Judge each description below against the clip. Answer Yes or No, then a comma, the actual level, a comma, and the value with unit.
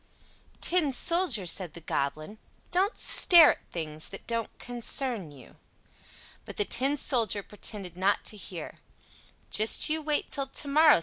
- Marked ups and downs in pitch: Yes, wide, 8.0 semitones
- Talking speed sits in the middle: Yes, average, 150 wpm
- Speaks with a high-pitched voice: Yes, high, 230 Hz